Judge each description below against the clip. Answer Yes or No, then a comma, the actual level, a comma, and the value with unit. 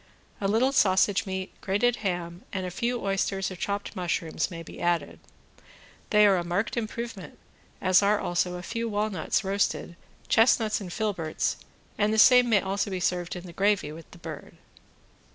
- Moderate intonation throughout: Yes, average, 3.1 semitones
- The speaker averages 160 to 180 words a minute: Yes, average, 170 wpm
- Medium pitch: No, high, 195 Hz